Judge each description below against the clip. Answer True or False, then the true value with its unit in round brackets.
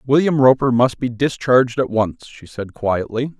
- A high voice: False (125 Hz)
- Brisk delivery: False (175 wpm)